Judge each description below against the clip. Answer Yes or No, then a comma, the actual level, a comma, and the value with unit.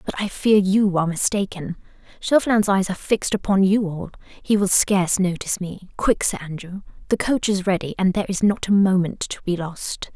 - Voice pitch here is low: No, high, 190 Hz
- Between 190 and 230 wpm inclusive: Yes, average, 195 wpm